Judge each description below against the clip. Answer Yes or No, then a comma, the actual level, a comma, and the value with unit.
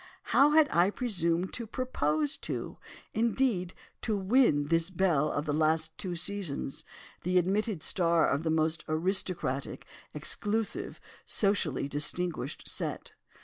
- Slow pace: Yes, slow, 115 wpm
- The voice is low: No, medium, 180 Hz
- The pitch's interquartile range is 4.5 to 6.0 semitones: Yes, average, 4.9 semitones